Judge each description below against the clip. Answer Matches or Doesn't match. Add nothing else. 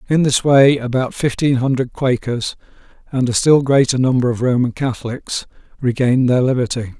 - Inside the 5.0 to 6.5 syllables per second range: Matches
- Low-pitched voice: Matches